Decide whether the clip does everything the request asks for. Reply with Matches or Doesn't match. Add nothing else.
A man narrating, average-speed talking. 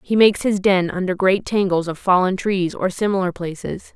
Doesn't match